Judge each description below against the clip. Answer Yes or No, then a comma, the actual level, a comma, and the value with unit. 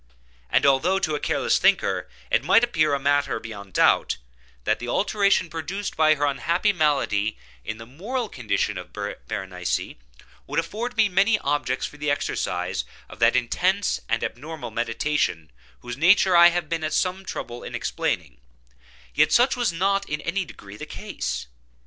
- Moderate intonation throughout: No, wide, 7.8 semitones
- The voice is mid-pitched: Yes, medium, 155 Hz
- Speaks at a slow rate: No, average, 165 wpm